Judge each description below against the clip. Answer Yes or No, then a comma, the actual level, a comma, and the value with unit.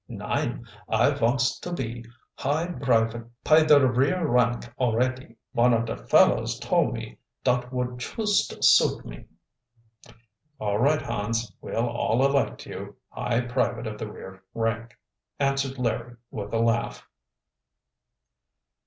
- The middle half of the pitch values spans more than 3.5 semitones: No, average, 2.9 semitones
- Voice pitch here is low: Yes, low, 120 Hz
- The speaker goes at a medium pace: No, slow, 130 wpm